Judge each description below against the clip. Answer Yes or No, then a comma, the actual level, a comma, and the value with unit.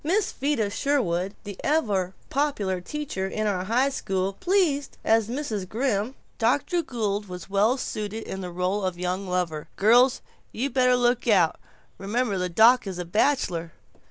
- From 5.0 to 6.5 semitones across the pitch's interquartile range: Yes, wide, 5.5 semitones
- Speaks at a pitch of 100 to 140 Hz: No, high, 215 Hz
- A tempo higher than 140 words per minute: Yes, average, 155 wpm